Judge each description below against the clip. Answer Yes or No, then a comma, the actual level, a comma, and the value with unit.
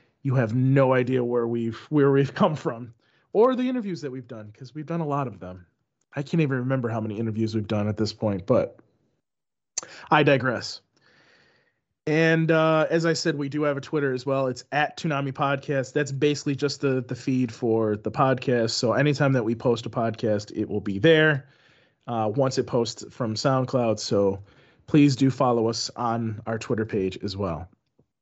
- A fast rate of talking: No, average, 195 wpm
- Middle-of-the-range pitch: No, low, 130 Hz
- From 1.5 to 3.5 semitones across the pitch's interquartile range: No, average, 4.3 semitones